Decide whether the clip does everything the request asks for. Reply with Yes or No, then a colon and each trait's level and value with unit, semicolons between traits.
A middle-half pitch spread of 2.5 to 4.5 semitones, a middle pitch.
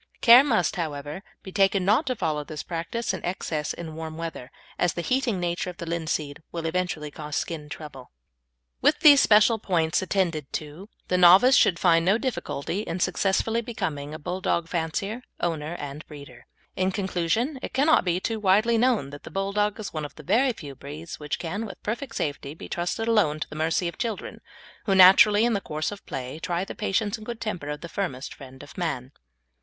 No: average, 5.2 semitones; medium, 175 Hz